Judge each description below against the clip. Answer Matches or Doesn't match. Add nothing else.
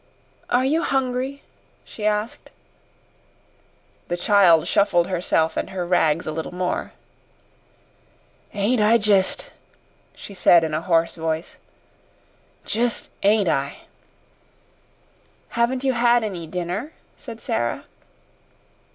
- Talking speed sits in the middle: Doesn't match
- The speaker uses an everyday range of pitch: Doesn't match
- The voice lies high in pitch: Matches